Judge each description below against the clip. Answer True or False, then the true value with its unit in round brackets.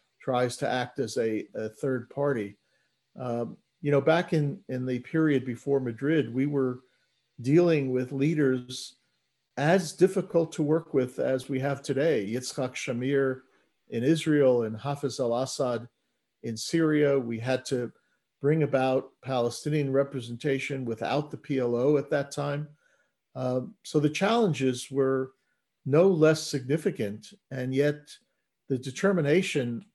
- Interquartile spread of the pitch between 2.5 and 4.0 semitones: True (2.8 semitones)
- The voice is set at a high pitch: False (135 Hz)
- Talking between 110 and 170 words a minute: True (135 wpm)